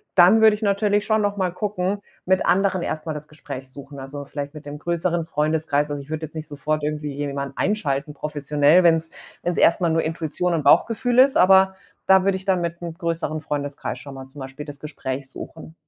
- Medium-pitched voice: Yes, medium, 160 Hz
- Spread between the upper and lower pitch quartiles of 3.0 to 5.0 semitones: Yes, average, 4.2 semitones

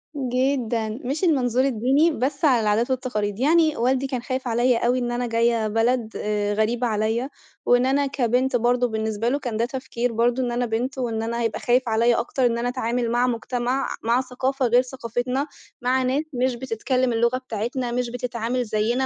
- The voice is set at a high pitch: Yes, high, 245 Hz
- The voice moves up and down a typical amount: No, narrow, 2.0 semitones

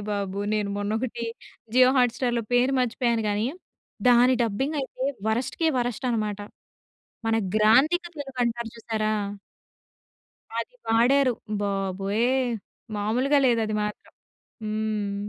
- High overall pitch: Yes, high, 230 Hz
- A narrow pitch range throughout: No, average, 3.0 semitones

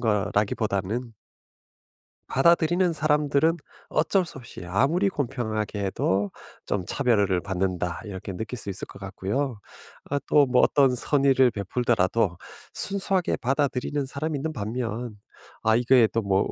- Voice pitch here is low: Yes, low, 120 Hz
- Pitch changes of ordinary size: No, wide, 5.9 semitones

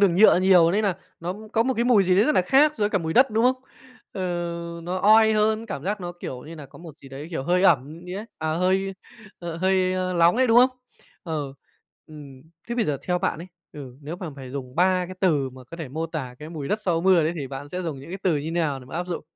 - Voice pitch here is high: No, medium, 175 Hz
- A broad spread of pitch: No, average, 4.3 semitones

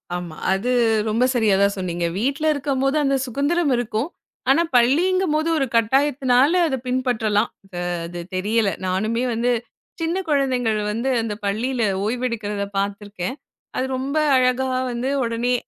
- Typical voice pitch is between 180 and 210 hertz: No, high, 245 Hz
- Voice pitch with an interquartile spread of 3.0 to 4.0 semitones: No, average, 4.4 semitones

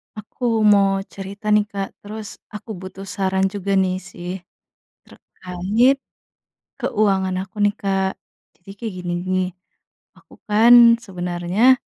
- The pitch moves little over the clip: Yes, narrow, 2.2 semitones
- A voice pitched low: No, high, 195 Hz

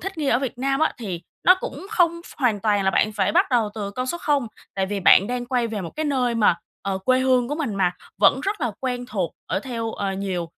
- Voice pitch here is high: Yes, high, 240 Hz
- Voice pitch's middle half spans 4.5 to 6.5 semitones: Yes, average, 5.1 semitones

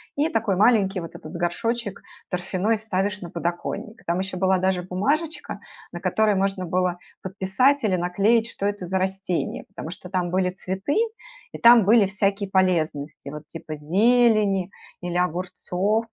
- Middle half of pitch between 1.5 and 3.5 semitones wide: Yes, average, 3.0 semitones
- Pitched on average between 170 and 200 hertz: Yes, high, 190 Hz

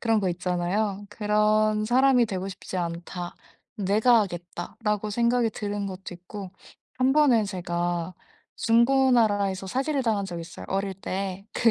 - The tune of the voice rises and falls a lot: No, average, 3.6 semitones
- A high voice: Yes, high, 205 Hz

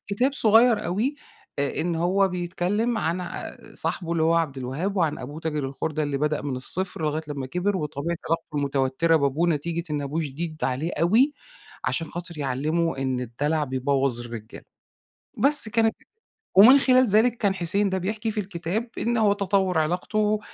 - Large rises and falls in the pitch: Yes, wide, 5.7 semitones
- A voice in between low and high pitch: Yes, medium, 170 Hz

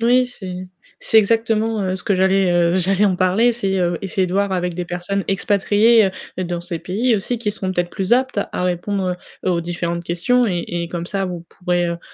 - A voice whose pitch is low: No, high, 190 Hz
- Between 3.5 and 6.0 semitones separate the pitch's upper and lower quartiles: No, average, 2.8 semitones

